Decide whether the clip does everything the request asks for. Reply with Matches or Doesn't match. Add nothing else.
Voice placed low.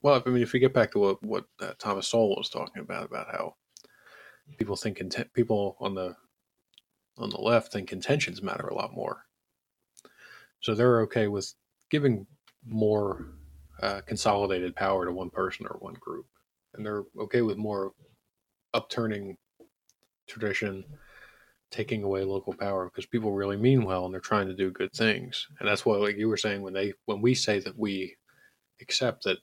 Matches